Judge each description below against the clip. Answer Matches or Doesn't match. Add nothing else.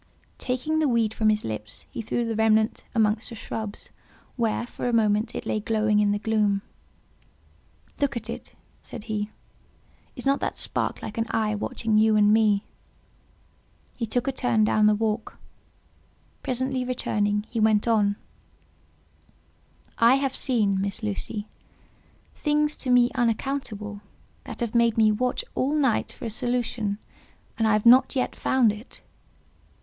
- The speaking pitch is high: Matches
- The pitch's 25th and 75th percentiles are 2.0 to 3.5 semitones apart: Matches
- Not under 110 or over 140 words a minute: Doesn't match